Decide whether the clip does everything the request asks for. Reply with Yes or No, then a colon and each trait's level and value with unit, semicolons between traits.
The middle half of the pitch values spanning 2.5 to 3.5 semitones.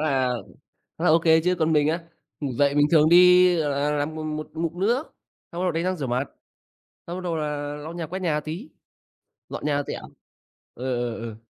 Yes: average, 2.9 semitones